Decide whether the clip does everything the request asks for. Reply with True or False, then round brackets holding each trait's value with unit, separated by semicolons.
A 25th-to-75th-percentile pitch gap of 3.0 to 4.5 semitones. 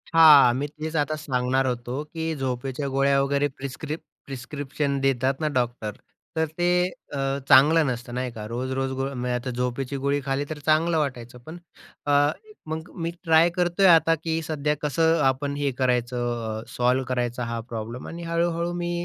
True (4.0 semitones)